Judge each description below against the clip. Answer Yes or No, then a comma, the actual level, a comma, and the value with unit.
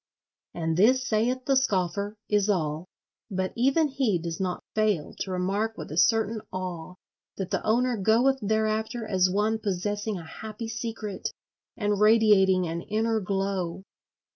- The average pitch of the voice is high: Yes, high, 210 Hz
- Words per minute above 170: No, average, 145 wpm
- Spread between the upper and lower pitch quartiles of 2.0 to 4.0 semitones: Yes, average, 3.2 semitones